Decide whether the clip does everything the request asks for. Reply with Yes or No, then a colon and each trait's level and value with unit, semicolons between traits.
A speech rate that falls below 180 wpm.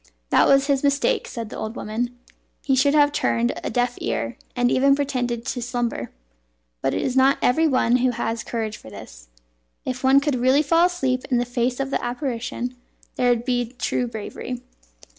No: average, 190 wpm